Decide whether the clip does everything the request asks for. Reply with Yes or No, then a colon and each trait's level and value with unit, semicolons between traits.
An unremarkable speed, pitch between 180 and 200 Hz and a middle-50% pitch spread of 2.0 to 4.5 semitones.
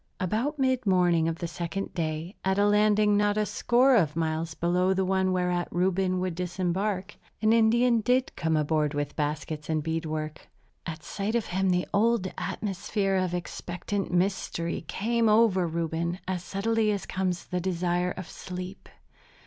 Yes: average, 165 wpm; medium, 185 Hz; average, 3.4 semitones